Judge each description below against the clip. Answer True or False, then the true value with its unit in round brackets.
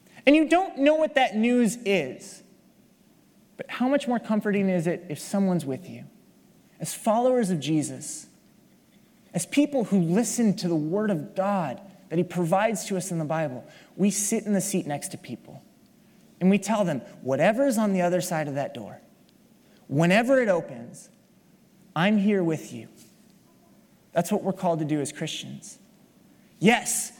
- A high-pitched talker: True (200 Hz)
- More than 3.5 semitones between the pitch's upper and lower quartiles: True (4.2 semitones)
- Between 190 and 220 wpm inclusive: False (170 wpm)